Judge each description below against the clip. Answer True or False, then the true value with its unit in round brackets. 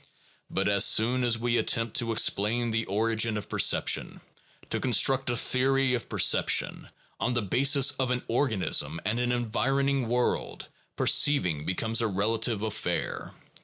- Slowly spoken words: False (150 wpm)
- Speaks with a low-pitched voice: True (115 Hz)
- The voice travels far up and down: False (2.6 semitones)